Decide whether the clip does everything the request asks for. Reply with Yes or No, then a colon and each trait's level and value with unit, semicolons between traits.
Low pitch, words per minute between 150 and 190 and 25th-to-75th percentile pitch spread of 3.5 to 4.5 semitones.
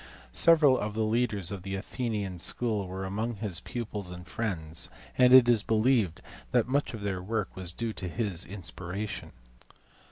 Yes: low, 105 Hz; average, 165 wpm; average, 3.9 semitones